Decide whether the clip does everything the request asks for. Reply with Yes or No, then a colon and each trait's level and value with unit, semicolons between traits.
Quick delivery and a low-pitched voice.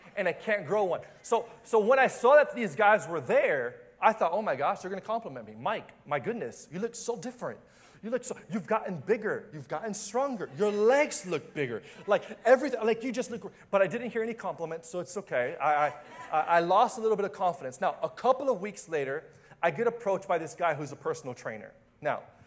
No: fast, 230 wpm; high, 210 Hz